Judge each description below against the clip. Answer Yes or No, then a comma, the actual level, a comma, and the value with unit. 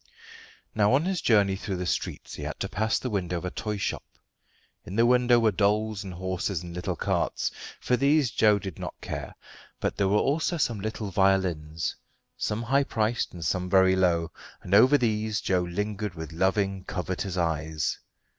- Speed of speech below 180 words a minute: No, average, 185 wpm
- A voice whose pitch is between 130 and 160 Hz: No, low, 100 Hz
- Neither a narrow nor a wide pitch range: Yes, average, 3.4 semitones